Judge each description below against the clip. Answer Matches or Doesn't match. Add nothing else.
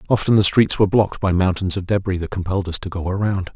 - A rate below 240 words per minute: Doesn't match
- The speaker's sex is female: Doesn't match